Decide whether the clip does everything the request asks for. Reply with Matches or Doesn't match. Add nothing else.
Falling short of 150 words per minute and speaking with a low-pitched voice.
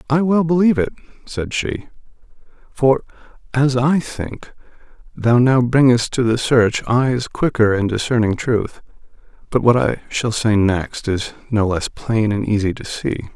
Doesn't match